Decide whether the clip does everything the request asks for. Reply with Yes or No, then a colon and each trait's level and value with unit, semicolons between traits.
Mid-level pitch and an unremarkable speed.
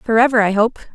No: high, 225 Hz; average, 190 wpm